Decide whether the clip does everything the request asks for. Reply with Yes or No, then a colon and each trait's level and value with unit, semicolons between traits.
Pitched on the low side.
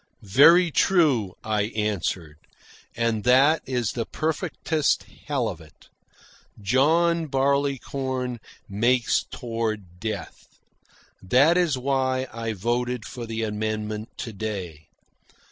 Yes: low, 120 Hz